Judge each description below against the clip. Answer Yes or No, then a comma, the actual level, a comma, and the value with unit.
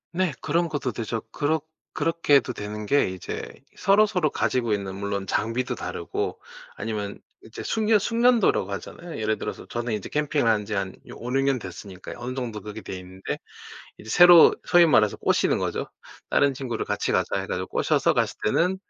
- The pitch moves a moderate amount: No, wide, 7.4 semitones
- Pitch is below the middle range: Yes, low, 125 Hz